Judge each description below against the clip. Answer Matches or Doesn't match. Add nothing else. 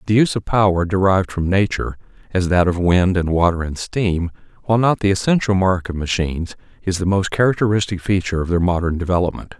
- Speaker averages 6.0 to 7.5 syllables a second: Matches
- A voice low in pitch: Matches